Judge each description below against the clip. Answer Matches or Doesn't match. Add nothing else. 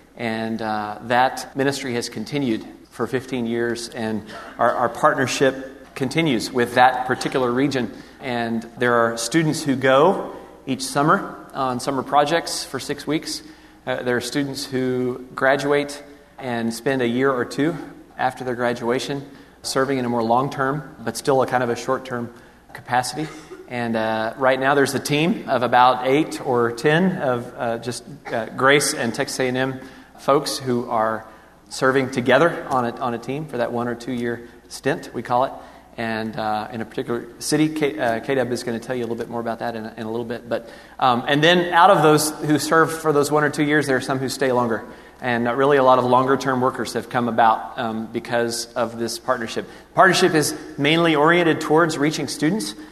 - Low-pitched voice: Matches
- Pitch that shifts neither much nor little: Matches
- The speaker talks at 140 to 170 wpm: Doesn't match